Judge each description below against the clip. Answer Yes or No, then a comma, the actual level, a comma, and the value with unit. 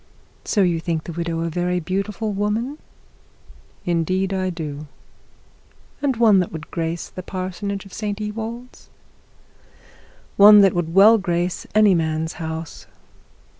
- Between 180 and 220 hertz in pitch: Yes, medium, 185 Hz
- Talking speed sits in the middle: No, slow, 130 wpm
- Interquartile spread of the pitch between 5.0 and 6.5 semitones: No, average, 3.8 semitones